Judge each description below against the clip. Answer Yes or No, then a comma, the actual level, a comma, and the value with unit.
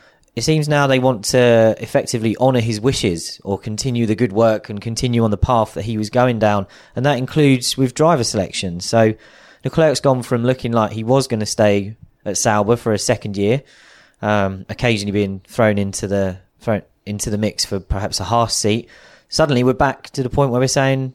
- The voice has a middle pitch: No, low, 115 Hz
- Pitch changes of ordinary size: Yes, average, 3.7 semitones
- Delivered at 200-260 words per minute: Yes, fast, 205 wpm